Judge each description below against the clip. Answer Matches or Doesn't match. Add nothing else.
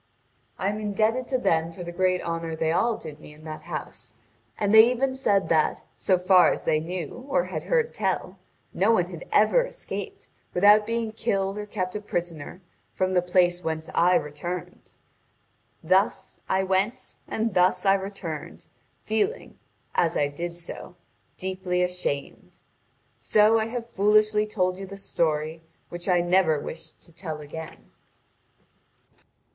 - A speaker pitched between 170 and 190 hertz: Matches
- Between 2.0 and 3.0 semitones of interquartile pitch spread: Doesn't match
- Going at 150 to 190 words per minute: Matches